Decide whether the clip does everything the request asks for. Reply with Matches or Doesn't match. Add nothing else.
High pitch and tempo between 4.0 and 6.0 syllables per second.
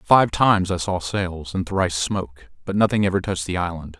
Doesn't match